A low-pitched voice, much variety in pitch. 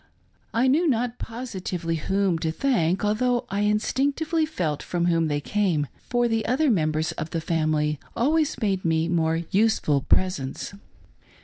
No: high, 195 Hz; wide, 7.1 semitones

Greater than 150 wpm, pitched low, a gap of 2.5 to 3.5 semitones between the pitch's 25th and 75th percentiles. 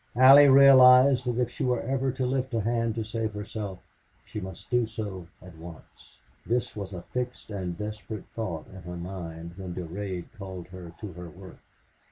No: average, 185 wpm; low, 105 Hz; average, 5.2 semitones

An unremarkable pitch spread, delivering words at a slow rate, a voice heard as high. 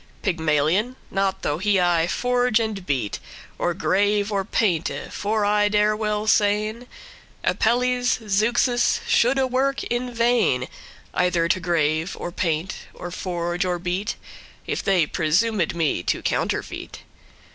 Yes: average, 4.6 semitones; slow, 130 wpm; high, 200 Hz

